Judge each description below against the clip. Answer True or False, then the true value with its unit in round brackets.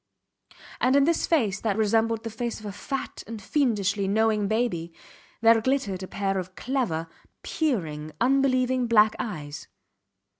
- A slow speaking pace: False (145 wpm)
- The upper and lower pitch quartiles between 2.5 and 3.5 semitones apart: False (4.4 semitones)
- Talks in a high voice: True (220 Hz)